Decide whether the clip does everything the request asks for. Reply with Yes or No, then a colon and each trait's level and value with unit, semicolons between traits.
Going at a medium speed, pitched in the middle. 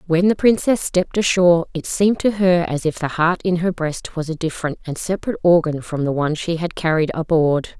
No: fast, 225 wpm; medium, 170 Hz